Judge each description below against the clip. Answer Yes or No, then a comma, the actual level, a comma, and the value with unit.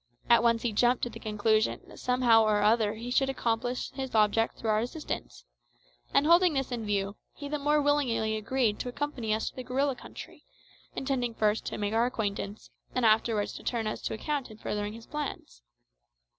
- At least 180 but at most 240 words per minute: Yes, average, 195 wpm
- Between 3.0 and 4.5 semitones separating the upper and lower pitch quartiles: Yes, average, 3.4 semitones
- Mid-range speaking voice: No, high, 230 Hz